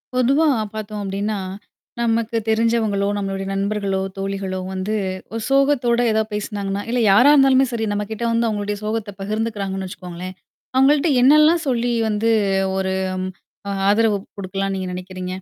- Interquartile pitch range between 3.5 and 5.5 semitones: No, average, 3.1 semitones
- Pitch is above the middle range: Yes, high, 210 Hz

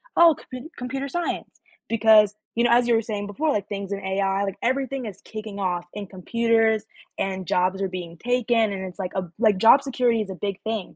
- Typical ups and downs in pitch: Yes, average, 3.7 semitones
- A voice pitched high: Yes, high, 215 Hz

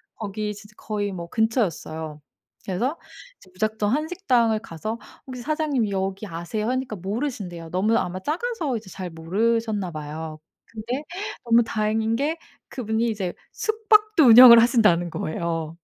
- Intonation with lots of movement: No, average, 5.0 semitones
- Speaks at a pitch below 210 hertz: No, high, 215 Hz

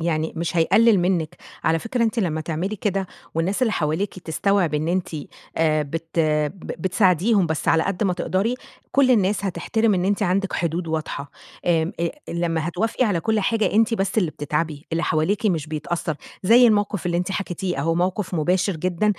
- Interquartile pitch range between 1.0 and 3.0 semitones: No, average, 3.9 semitones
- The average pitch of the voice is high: No, medium, 180 Hz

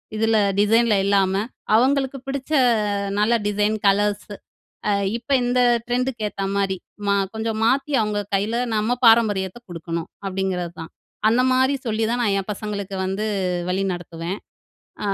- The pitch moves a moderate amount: Yes, average, 3.4 semitones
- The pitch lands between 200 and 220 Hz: Yes, high, 210 Hz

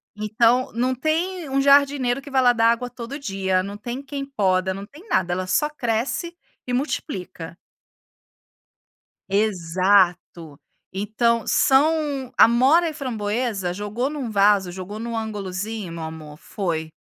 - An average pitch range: No, wide, 6.0 semitones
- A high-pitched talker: Yes, high, 225 Hz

